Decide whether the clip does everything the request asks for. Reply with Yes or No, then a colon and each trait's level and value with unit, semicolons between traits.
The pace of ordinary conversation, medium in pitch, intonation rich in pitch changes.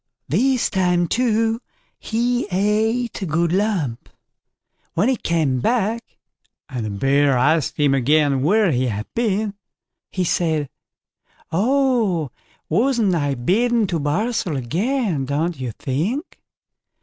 No: slow, 120 wpm; medium, 180 Hz; wide, 7.8 semitones